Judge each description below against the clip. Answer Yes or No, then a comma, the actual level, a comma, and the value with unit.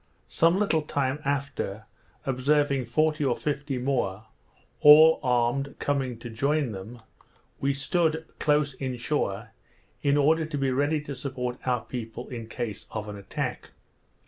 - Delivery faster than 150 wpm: No, average, 145 wpm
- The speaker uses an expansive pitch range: No, average, 3.4 semitones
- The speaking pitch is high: No, low, 135 Hz